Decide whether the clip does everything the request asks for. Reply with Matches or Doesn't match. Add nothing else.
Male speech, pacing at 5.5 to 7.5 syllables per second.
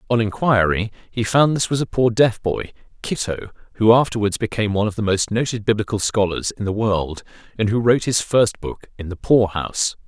Matches